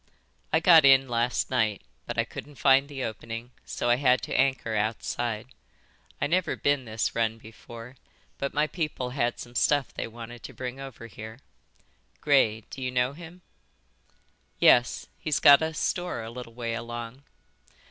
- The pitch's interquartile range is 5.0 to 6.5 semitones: No, average, 3.3 semitones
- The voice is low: Yes, low, 125 Hz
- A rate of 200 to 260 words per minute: No, average, 160 wpm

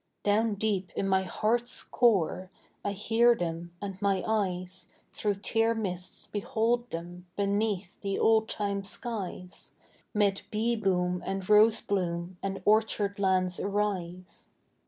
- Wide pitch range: No, average, 2.8 semitones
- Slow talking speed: Yes, slow, 130 wpm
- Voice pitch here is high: Yes, high, 200 Hz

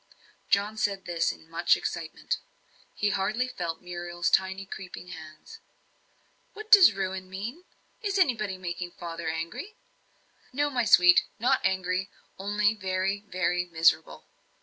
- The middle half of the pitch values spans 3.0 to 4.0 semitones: Yes, average, 3.4 semitones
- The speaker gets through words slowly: Yes, slow, 125 wpm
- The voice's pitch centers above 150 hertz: Yes, high, 190 Hz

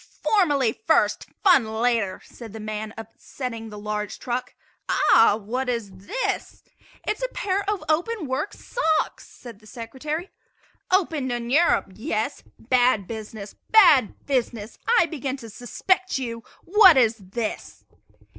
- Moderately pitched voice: No, high, 245 Hz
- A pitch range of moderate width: No, wide, 6.3 semitones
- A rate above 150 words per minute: No, slow, 135 wpm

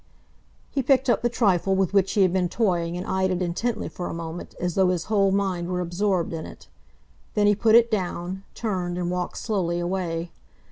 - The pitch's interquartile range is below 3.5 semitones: Yes, average, 2.8 semitones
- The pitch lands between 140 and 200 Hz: Yes, medium, 185 Hz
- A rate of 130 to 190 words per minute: No, fast, 205 wpm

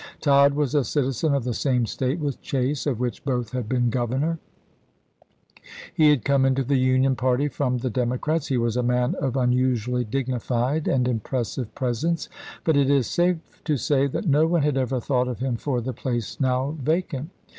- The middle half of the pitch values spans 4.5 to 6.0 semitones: No, narrow, 2.4 semitones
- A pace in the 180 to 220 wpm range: Yes, average, 190 wpm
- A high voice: No, low, 130 Hz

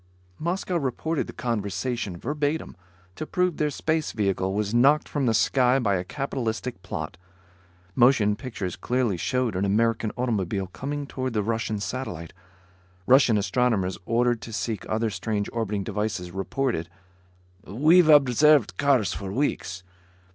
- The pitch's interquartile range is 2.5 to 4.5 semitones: No, average, 5.1 semitones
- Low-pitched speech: Yes, low, 115 Hz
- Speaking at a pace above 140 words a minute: No, slow, 135 wpm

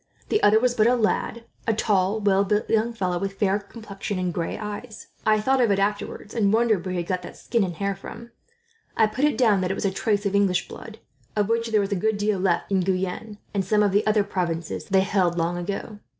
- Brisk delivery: Yes, fast, 245 wpm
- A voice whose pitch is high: Yes, high, 205 Hz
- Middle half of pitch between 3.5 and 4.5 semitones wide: No, narrow, 2.4 semitones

